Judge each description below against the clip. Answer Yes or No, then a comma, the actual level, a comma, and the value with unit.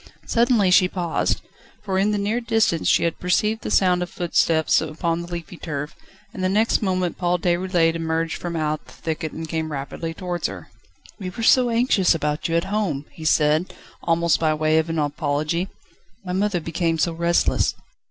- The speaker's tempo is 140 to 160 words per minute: No, average, 185 wpm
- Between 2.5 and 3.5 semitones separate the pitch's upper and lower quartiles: Yes, average, 2.8 semitones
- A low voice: No, medium, 170 Hz